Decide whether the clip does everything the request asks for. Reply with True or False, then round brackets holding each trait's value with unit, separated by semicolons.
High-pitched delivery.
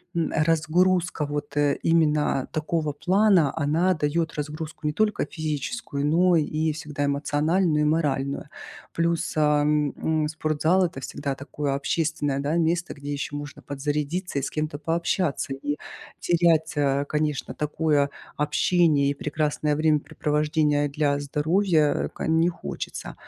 False (150 Hz)